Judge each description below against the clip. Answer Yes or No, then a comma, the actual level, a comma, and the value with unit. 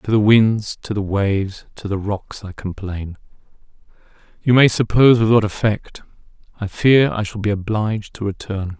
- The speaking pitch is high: No, low, 105 Hz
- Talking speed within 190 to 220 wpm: No, average, 165 wpm